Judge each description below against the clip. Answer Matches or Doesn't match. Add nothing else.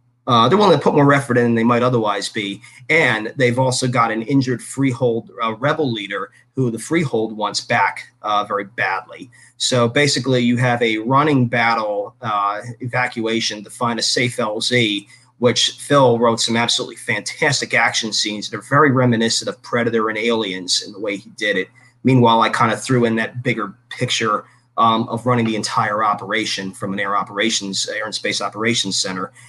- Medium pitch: Doesn't match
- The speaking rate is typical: Matches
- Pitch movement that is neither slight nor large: Doesn't match